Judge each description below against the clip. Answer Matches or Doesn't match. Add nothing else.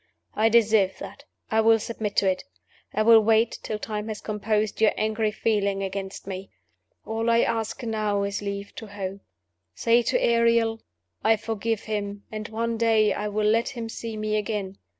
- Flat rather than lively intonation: Matches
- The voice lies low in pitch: Doesn't match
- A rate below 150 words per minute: Doesn't match